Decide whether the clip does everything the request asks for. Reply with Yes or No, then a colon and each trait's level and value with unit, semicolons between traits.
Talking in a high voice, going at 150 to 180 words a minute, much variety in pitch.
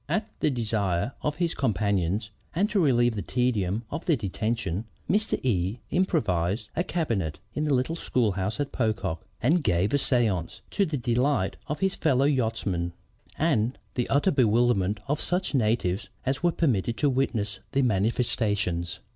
No: low, 120 Hz; average, 155 wpm; wide, 6.1 semitones